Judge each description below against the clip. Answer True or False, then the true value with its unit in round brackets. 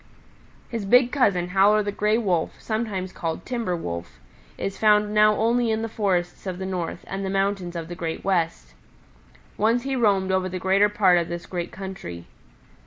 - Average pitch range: True (3.2 semitones)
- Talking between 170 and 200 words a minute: True (180 wpm)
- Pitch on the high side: True (195 Hz)